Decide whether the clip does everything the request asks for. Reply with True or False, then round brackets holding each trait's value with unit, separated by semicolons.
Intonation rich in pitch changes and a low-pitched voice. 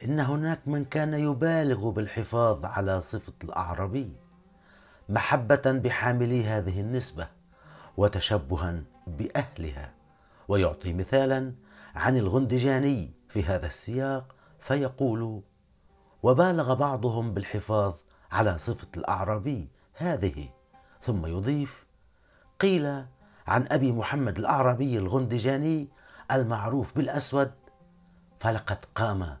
True (6.1 semitones; 115 Hz)